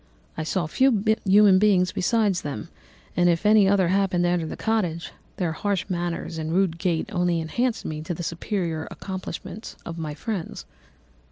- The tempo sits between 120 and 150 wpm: No, average, 170 wpm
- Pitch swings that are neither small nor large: Yes, average, 3.2 semitones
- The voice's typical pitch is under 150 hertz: No, medium, 180 Hz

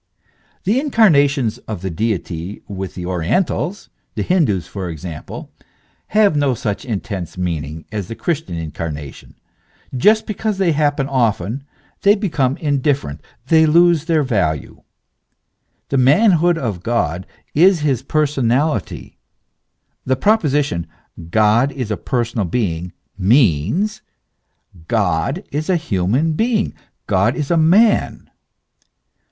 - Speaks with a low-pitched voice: Yes, low, 130 Hz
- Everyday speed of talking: No, slow, 120 wpm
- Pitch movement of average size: No, wide, 8.9 semitones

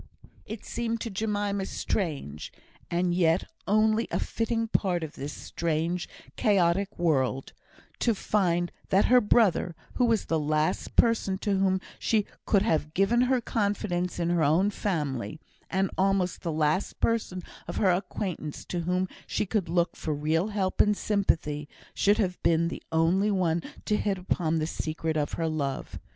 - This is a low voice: No, medium, 180 Hz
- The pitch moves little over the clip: No, average, 4.2 semitones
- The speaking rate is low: No, average, 160 wpm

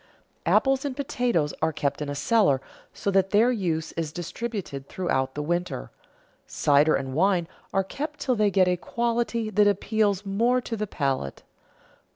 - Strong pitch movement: Yes, wide, 6.8 semitones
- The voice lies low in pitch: No, high, 195 Hz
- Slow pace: No, average, 165 wpm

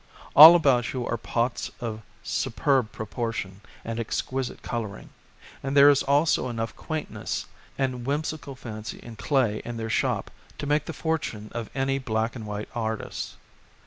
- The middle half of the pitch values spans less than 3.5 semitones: No, average, 3.8 semitones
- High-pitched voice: No, low, 120 Hz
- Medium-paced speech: Yes, average, 150 wpm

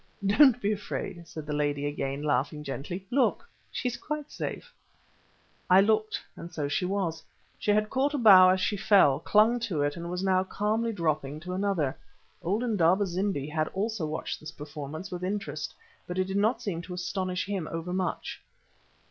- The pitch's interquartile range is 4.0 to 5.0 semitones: Yes, average, 4.7 semitones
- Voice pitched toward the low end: No, medium, 185 Hz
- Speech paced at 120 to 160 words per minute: No, average, 180 wpm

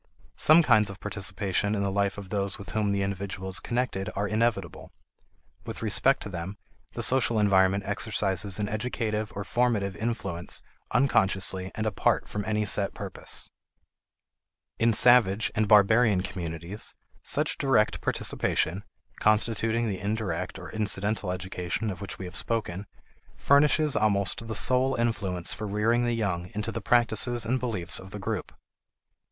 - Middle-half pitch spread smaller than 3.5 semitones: Yes, average, 2.9 semitones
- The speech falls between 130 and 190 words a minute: Yes, average, 150 wpm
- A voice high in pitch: No, low, 105 Hz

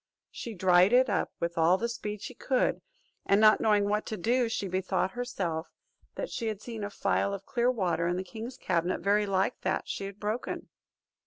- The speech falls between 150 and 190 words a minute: No, average, 200 wpm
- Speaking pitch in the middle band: No, high, 205 Hz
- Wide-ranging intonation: No, average, 3.4 semitones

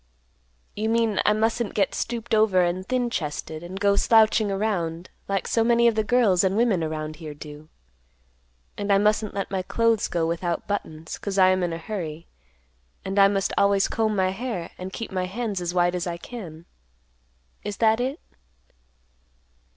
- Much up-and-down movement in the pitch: No, average, 4.0 semitones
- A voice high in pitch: Yes, high, 195 Hz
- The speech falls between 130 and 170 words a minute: No, average, 180 wpm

